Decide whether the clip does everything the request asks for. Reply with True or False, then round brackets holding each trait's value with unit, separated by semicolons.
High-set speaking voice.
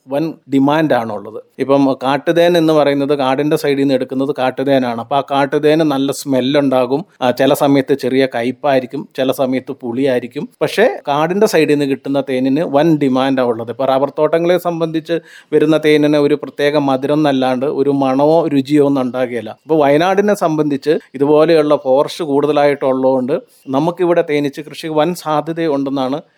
False (140 Hz)